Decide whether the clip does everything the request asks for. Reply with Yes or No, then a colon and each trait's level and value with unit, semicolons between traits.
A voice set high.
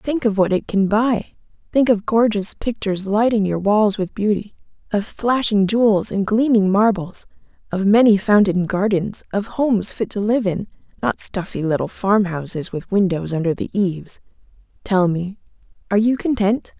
Yes: high, 205 Hz